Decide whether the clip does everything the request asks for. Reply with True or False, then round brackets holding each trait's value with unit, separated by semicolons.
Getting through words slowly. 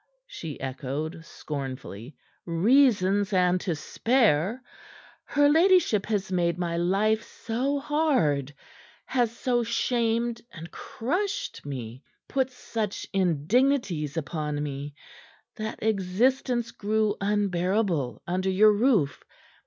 True (100 wpm)